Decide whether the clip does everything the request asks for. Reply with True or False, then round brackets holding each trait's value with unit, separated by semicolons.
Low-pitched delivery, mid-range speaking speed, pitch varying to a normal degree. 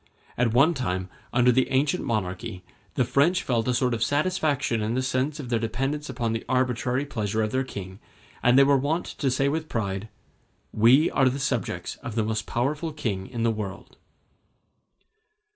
True (125 Hz; 180 wpm; 3.9 semitones)